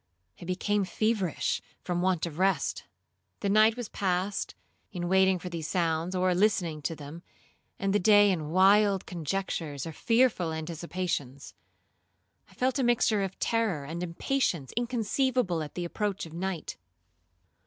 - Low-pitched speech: No, medium, 185 Hz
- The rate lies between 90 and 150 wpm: Yes, average, 145 wpm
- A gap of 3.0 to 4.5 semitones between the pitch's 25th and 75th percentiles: Yes, average, 3.7 semitones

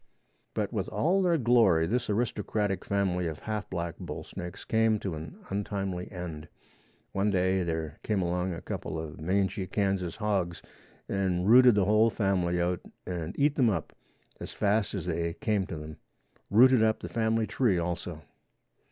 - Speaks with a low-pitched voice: Yes, very low, 95 Hz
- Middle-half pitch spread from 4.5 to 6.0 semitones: No, average, 3.9 semitones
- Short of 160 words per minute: No, average, 165 wpm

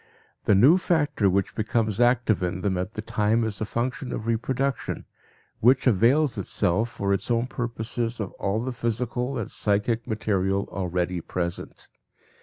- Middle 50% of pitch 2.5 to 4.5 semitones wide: Yes, average, 3.7 semitones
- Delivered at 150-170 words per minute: Yes, average, 155 wpm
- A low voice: Yes, low, 110 Hz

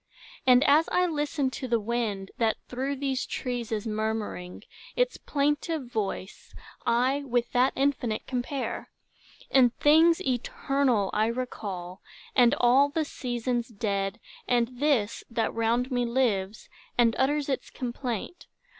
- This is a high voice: Yes, high, 245 Hz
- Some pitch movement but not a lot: Yes, average, 3.6 semitones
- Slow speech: Yes, slow, 130 wpm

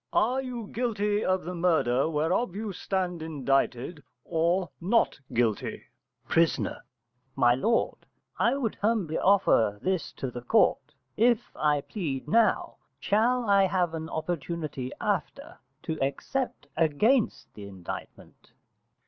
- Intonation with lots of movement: Yes, wide, 6.4 semitones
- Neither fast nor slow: No, slow, 125 wpm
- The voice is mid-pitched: Yes, medium, 175 Hz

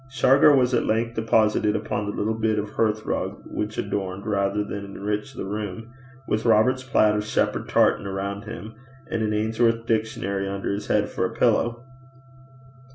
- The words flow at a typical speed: Yes, average, 165 wpm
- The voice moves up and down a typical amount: No, narrow, 1.9 semitones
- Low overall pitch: Yes, low, 110 Hz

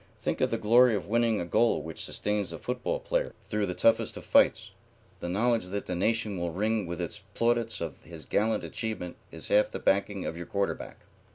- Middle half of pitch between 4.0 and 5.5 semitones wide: Yes, average, 4.4 semitones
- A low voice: Yes, low, 105 Hz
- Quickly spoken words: Yes, fast, 210 wpm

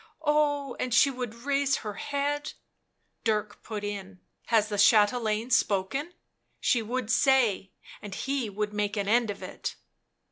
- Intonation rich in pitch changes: No, average, 4.5 semitones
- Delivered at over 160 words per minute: No, average, 150 wpm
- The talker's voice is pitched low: No, high, 230 Hz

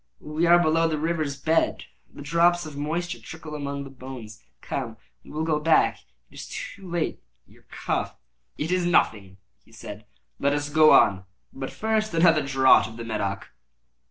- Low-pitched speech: No, medium, 150 Hz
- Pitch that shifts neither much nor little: Yes, average, 4.0 semitones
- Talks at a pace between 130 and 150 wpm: No, average, 180 wpm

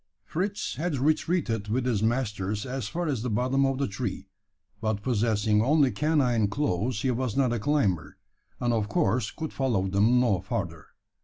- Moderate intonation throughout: Yes, average, 4.4 semitones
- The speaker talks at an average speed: Yes, average, 170 wpm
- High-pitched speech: No, low, 120 Hz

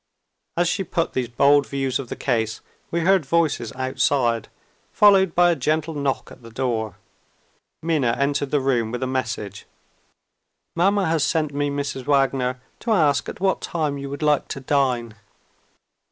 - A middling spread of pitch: Yes, average, 4.0 semitones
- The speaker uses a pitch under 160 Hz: Yes, medium, 140 Hz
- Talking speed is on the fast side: No, average, 165 wpm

